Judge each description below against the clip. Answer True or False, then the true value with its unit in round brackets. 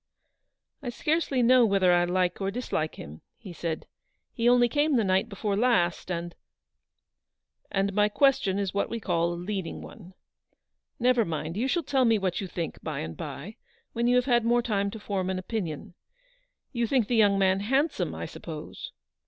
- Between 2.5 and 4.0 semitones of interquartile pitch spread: False (4.7 semitones)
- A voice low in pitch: False (205 Hz)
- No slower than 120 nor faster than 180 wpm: False (195 wpm)